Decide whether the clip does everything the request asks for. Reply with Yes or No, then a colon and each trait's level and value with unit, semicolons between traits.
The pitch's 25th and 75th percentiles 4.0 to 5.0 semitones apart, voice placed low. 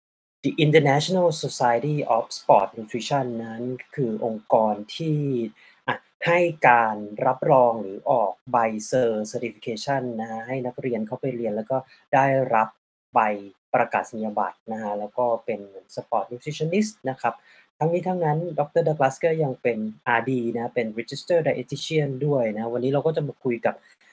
Yes: average, 4.5 semitones; low, 125 Hz